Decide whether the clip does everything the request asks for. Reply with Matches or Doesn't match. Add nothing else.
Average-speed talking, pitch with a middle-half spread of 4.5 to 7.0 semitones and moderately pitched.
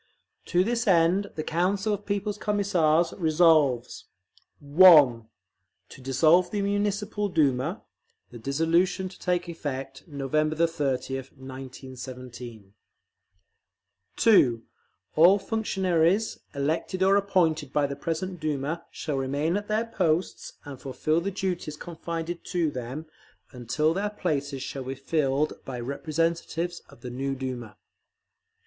Doesn't match